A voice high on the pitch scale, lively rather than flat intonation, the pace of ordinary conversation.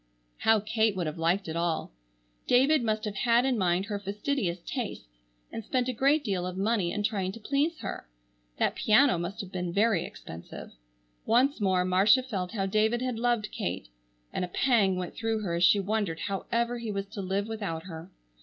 No: high, 205 Hz; average, 4.3 semitones; average, 195 wpm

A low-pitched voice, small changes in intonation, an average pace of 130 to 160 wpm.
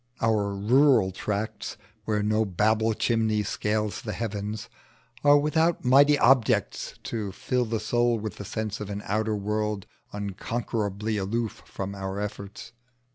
Yes: low, 110 Hz; narrow, 2.1 semitones; slow, 135 wpm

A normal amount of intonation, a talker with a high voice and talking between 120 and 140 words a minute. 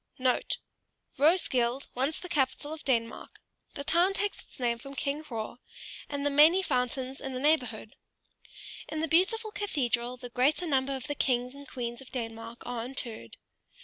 No: average, 3.8 semitones; very high, 265 Hz; average, 165 wpm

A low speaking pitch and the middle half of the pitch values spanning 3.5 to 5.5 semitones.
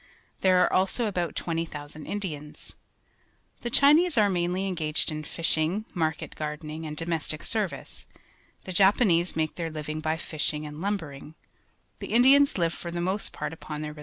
No: medium, 165 Hz; average, 3.9 semitones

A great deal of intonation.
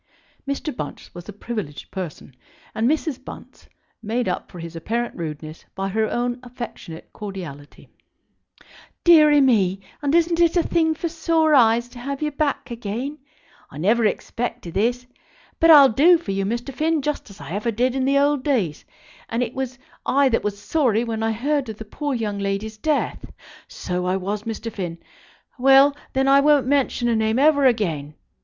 Yes: wide, 5.8 semitones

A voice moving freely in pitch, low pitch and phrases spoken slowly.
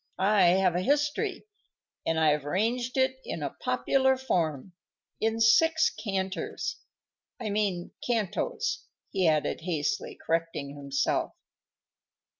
No: wide, 7.3 semitones; high, 195 Hz; slow, 110 wpm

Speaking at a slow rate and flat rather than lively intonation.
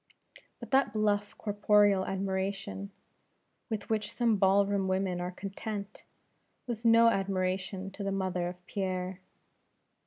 Yes: slow, 125 wpm; narrow, 1.6 semitones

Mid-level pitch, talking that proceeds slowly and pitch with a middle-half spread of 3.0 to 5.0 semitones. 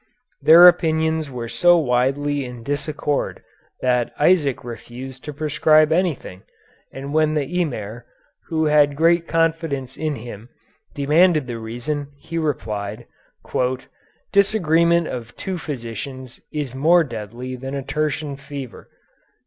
Yes: medium, 145 Hz; slow, 120 wpm; average, 4.2 semitones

